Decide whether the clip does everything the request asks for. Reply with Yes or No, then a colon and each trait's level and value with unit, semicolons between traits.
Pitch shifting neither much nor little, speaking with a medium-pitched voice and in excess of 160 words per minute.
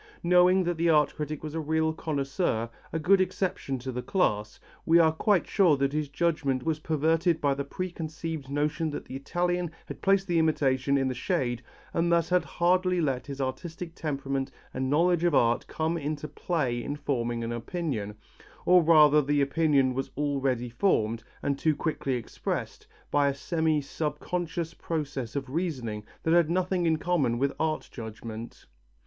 Yes: average, 4.0 semitones; medium, 150 Hz; average, 170 wpm